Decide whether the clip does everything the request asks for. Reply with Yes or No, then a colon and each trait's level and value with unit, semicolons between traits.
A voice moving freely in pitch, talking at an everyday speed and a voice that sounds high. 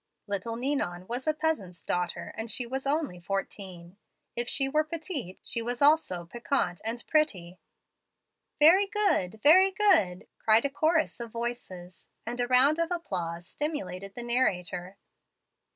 Yes: wide, 8.5 semitones; average, 150 wpm; high, 240 Hz